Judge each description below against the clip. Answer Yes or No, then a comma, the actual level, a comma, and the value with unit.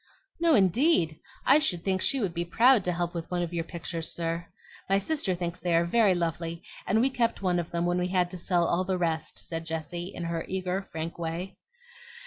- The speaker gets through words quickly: Yes, fast, 220 wpm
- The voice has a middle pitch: Yes, medium, 175 Hz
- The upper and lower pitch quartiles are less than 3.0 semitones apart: Yes, narrow, 2.4 semitones